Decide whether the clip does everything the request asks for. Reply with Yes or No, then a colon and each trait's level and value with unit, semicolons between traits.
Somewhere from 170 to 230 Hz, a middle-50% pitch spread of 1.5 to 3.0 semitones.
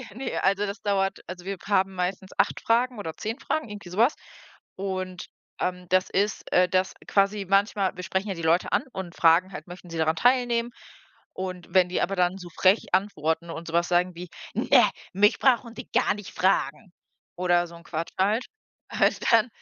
Yes: high, 190 Hz; narrow, 2.6 semitones